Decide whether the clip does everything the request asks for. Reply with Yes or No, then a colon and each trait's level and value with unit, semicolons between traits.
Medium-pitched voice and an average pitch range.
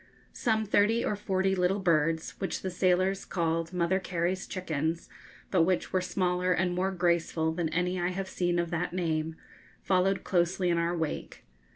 No: medium, 180 Hz; narrow, 1.9 semitones